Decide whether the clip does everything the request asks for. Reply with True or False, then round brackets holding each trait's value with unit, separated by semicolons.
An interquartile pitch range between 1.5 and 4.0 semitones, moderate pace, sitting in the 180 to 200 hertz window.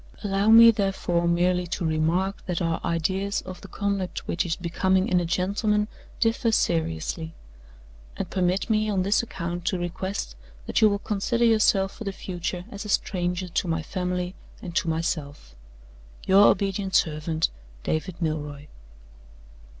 True (3.0 semitones; 150 wpm; 185 Hz)